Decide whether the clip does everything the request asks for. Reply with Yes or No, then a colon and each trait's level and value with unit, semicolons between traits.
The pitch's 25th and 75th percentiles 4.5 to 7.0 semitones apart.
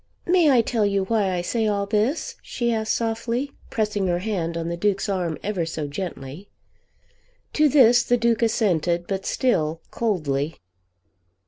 Yes: average, 5.0 semitones